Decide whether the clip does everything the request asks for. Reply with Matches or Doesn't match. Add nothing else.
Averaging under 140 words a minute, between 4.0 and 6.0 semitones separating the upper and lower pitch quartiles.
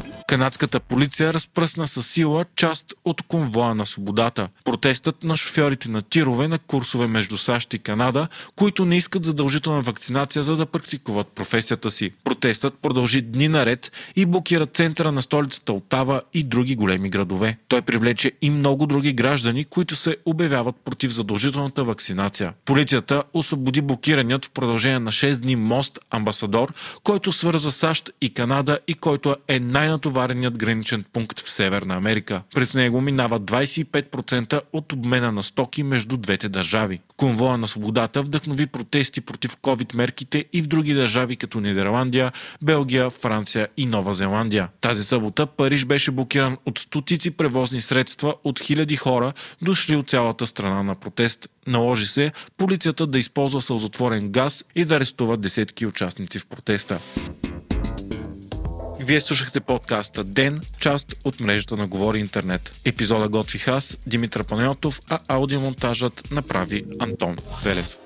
Doesn't match